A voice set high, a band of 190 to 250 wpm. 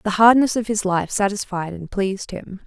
Yes: high, 200 Hz; fast, 205 wpm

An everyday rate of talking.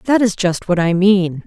No: fast, 245 wpm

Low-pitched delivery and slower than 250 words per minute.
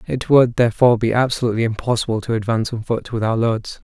Yes: low, 115 Hz; average, 200 wpm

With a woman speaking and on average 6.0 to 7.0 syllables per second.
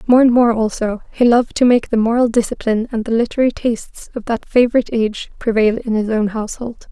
Yes: female; 6.3 syllables/s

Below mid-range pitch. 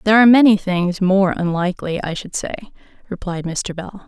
No: high, 190 Hz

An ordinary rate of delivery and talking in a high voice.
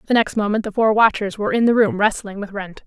No: fast, 270 wpm; high, 210 Hz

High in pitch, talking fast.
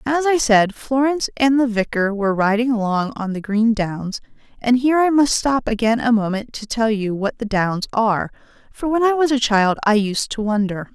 Yes: high, 230 Hz; fast, 215 wpm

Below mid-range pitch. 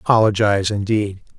Yes: low, 105 Hz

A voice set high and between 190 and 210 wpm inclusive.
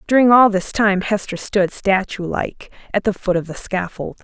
Yes: high, 200 Hz; average, 200 wpm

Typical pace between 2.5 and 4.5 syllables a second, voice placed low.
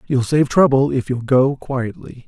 Yes: 4.4 syllables/s; low, 130 Hz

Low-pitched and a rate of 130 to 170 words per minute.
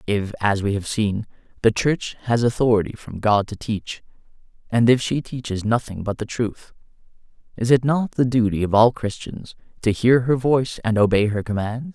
No: low, 115 Hz; average, 185 wpm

